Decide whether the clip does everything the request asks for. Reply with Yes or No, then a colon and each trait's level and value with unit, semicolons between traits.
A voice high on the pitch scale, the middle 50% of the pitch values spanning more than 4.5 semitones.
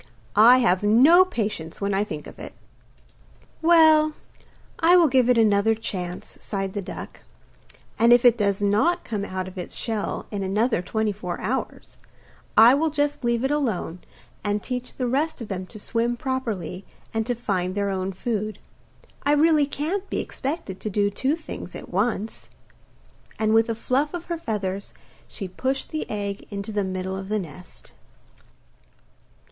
Yes: high, 220 Hz; average, 5.0 semitones